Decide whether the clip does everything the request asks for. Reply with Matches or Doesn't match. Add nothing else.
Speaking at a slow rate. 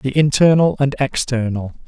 Matches